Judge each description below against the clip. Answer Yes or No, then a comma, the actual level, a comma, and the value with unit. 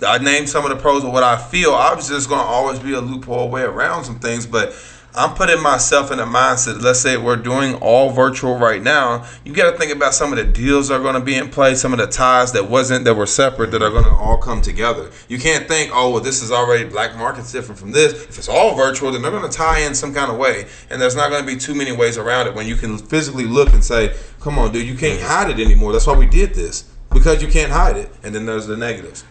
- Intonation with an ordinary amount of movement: Yes, average, 3.2 semitones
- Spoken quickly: Yes, fast, 270 wpm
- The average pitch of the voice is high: No, low, 130 Hz